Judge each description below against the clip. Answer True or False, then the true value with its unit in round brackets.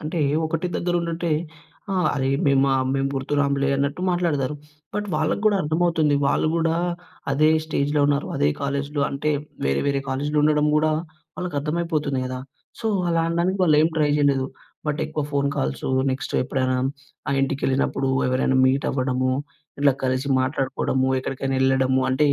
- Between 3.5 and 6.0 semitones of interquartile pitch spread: False (2.8 semitones)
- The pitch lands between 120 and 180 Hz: True (140 Hz)